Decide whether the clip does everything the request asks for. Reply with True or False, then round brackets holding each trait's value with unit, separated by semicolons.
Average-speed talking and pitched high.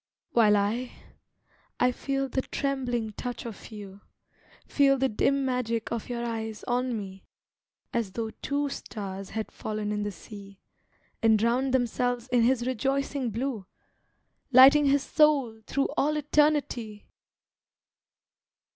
False (130 wpm; 240 Hz)